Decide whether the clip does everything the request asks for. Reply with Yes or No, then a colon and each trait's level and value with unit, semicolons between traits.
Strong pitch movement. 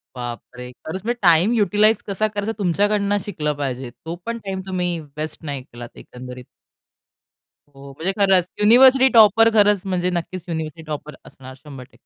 Yes: wide, 6.2 semitones